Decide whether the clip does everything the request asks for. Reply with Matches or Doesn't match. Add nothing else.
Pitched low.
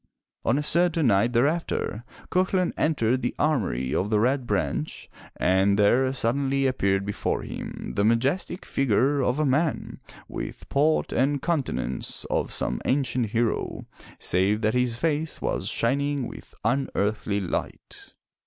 Matches